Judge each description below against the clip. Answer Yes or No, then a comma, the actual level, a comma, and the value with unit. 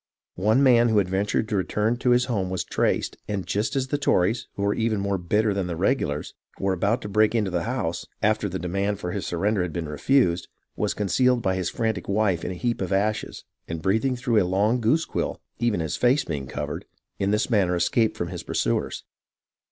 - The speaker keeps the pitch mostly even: No, average, 3.9 semitones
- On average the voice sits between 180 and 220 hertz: No, low, 100 Hz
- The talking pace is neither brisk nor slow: No, fast, 215 wpm